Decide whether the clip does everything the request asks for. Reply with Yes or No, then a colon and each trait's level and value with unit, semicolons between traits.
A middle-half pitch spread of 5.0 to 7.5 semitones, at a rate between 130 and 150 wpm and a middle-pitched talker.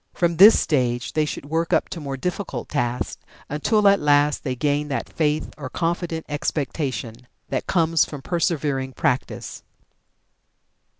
No: average, 3.6 semitones; average, 140 wpm; medium, 150 Hz